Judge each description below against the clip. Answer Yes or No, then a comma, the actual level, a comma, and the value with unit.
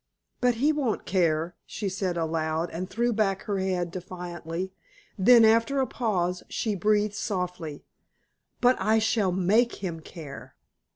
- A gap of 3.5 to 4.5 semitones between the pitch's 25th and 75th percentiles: Yes, average, 4.1 semitones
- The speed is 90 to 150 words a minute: Yes, average, 140 wpm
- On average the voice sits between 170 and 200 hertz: Yes, high, 190 Hz